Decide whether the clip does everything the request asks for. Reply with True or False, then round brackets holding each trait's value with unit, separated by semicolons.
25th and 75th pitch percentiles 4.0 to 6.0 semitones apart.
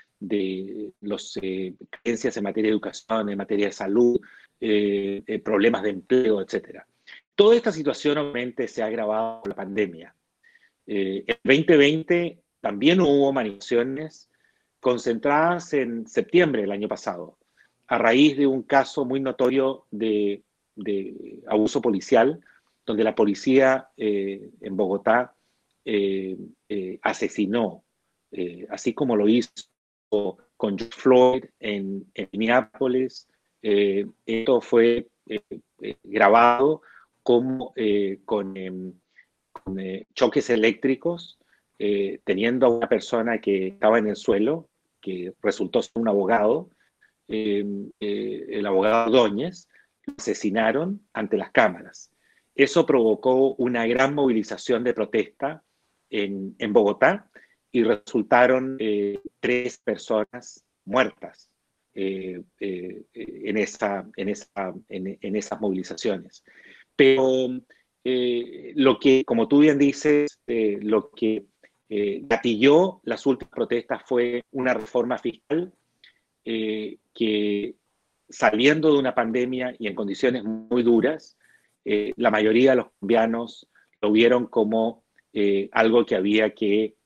True (4.3 semitones)